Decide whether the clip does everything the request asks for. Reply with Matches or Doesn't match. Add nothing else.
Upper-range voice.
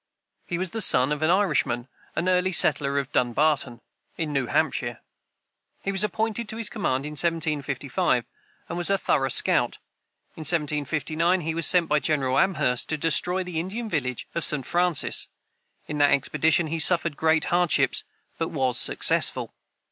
Doesn't match